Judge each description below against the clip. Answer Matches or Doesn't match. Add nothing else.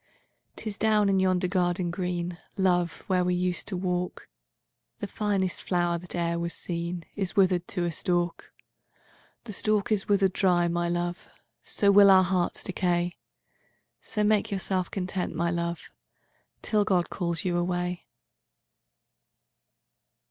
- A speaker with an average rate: Doesn't match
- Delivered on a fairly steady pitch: Matches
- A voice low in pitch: Doesn't match